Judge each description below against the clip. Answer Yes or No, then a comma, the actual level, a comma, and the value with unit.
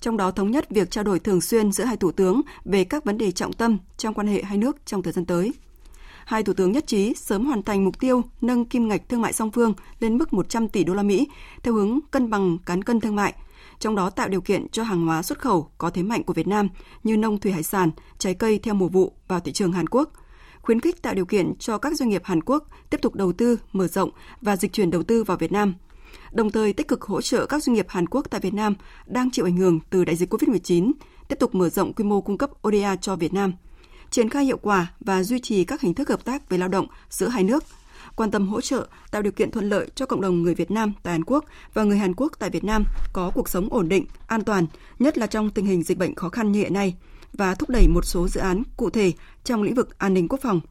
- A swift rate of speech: Yes, fast, 270 wpm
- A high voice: Yes, high, 205 Hz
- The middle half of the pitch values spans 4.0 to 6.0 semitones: Yes, average, 4.3 semitones